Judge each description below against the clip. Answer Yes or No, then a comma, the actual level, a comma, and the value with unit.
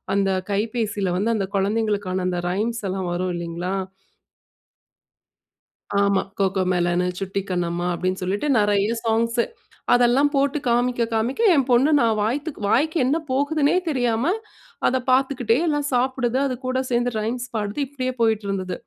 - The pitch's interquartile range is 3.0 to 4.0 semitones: No, average, 4.8 semitones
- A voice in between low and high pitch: No, high, 225 Hz